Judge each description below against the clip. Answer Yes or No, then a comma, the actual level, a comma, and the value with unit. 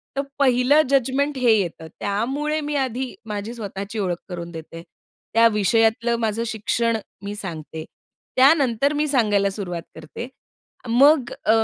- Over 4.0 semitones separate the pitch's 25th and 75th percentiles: Yes, average, 4.7 semitones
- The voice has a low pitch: No, high, 230 Hz